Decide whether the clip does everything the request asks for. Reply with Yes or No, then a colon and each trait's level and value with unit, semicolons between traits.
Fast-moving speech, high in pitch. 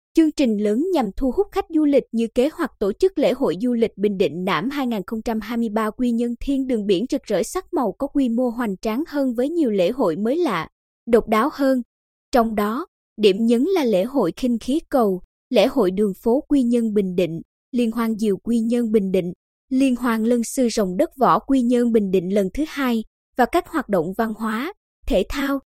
No: average, 215 wpm; high, 240 Hz